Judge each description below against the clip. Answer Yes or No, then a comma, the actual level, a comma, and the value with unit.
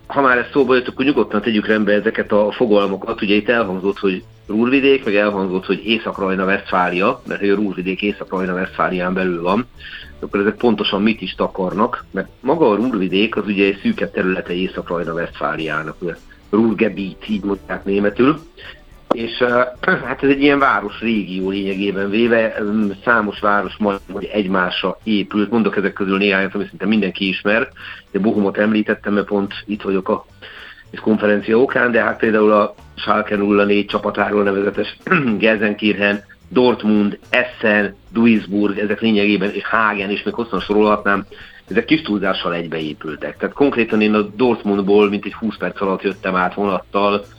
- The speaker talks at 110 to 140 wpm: No, average, 150 wpm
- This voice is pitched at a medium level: No, low, 105 Hz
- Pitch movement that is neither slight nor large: No, narrow, 1.8 semitones